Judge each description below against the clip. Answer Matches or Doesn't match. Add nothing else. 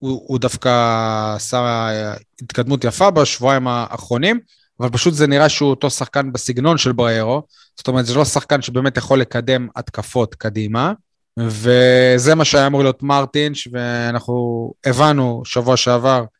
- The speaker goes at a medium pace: Matches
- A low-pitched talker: Matches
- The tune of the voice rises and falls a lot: Doesn't match